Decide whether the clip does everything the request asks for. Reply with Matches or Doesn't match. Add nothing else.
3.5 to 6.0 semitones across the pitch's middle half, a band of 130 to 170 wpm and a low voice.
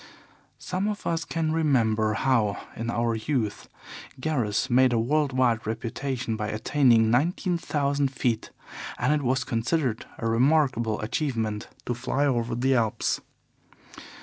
Matches